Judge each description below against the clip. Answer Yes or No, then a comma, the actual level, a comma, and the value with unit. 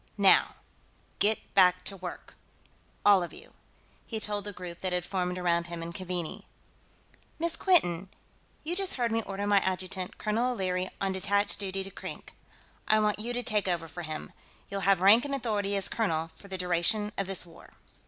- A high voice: Yes, high, 195 Hz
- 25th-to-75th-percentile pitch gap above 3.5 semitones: No, average, 2.8 semitones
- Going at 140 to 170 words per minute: No, average, 185 wpm